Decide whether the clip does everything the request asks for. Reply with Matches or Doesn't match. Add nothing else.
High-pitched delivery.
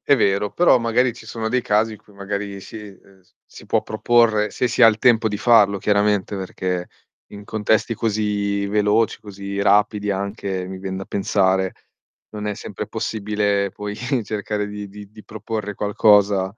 Doesn't match